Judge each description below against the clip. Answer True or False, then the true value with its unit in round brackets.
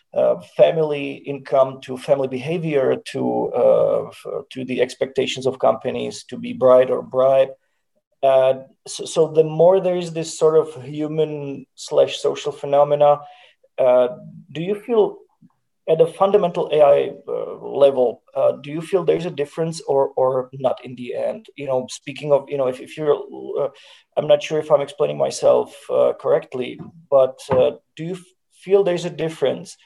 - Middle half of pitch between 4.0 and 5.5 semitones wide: True (5.2 semitones)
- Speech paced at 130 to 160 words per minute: False (170 wpm)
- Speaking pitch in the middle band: True (155 Hz)